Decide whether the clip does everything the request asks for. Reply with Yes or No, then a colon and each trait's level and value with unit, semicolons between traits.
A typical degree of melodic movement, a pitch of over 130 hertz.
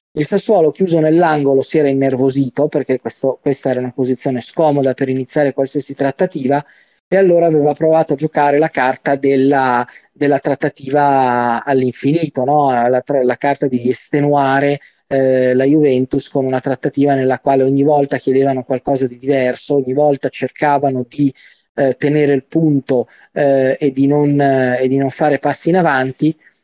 No: narrow, 1.9 semitones; medium, 140 Hz